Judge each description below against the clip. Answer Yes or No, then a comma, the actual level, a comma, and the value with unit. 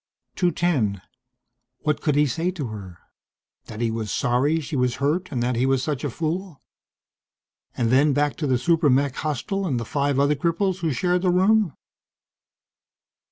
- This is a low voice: No, medium, 145 Hz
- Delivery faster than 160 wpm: Yes, average, 170 wpm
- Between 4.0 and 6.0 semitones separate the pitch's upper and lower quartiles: Yes, average, 5.0 semitones